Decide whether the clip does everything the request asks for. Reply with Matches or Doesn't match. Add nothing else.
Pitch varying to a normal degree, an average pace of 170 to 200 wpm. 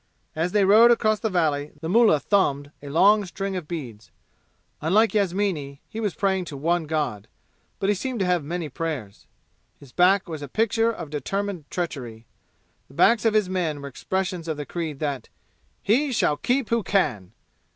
Doesn't match